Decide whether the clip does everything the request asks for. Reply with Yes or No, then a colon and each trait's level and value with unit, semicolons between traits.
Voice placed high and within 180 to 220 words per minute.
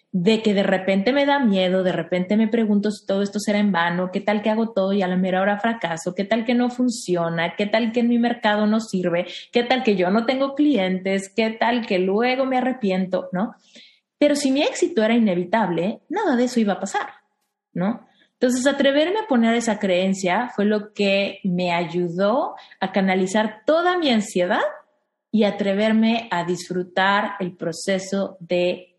Yes: high, 210 Hz; fast, 190 wpm